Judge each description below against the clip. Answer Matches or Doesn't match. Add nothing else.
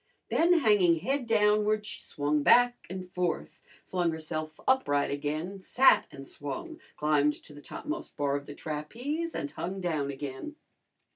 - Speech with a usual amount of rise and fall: Doesn't match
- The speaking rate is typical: Matches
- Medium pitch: Matches